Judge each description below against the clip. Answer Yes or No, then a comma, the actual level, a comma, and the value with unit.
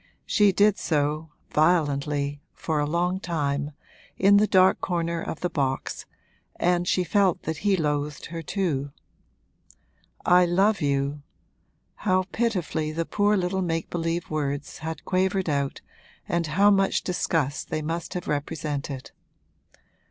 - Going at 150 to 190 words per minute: No, slow, 135 wpm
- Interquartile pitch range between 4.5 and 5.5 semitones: No, average, 3.9 semitones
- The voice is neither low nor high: Yes, medium, 165 Hz